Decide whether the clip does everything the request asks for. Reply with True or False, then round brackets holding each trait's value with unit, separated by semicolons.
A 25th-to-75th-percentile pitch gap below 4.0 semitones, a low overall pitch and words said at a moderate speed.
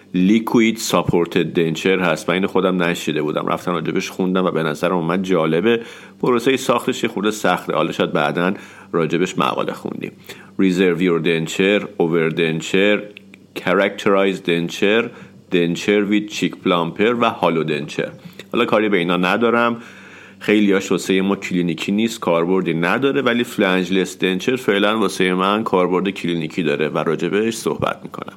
True (2.8 semitones; 95 Hz; 145 wpm)